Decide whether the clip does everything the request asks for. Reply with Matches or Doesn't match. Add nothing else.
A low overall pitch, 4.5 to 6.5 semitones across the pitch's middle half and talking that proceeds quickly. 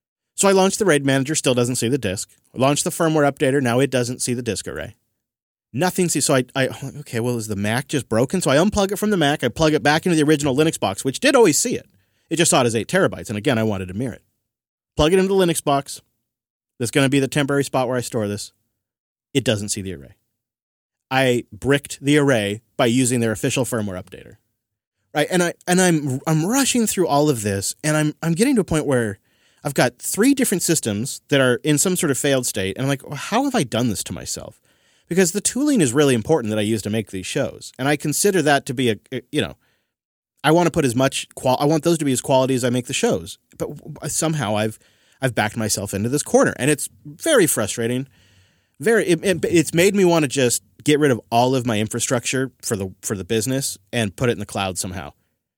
Matches